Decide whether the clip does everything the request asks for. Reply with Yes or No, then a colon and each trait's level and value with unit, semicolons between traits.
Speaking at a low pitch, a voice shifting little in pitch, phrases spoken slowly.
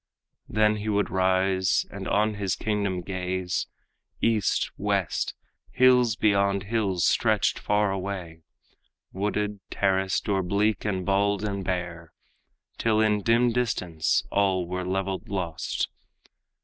Yes: low, 100 Hz; narrow, 2.1 semitones; slow, 120 wpm